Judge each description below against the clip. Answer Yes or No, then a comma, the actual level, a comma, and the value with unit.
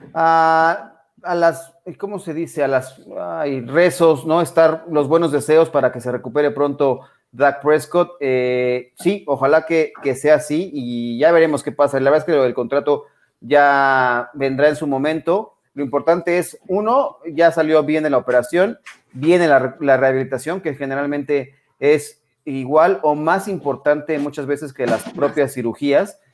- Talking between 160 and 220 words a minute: Yes, average, 165 wpm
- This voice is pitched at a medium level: Yes, medium, 150 Hz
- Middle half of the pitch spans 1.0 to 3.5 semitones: Yes, average, 3.1 semitones